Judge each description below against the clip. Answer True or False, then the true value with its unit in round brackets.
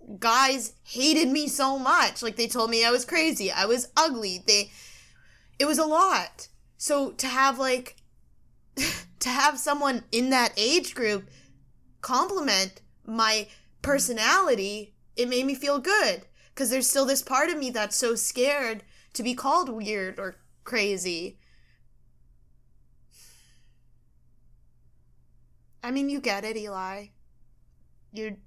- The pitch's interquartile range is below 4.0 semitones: False (5.5 semitones)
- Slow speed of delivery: True (130 wpm)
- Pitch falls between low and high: False (235 Hz)